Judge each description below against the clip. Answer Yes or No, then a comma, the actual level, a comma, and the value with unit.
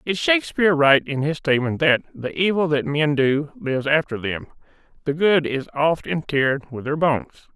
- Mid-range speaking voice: Yes, medium, 150 Hz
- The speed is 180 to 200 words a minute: Yes, average, 185 wpm